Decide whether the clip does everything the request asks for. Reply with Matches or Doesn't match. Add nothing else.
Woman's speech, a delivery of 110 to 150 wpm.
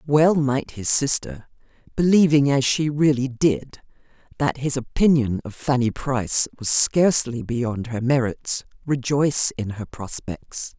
Matches